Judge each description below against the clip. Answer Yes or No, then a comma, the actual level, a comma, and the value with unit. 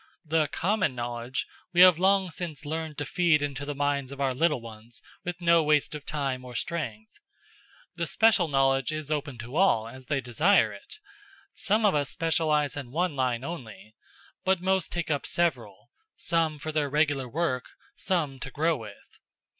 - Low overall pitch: No, medium, 145 Hz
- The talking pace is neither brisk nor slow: Yes, average, 175 wpm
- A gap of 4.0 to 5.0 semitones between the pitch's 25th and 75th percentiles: Yes, average, 4.5 semitones